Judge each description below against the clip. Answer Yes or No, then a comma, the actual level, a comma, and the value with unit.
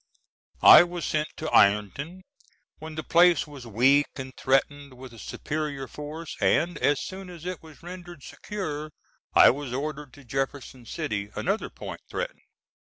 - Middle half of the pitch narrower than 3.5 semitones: No, average, 4.2 semitones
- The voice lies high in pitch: No, medium, 150 Hz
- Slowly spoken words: No, average, 155 wpm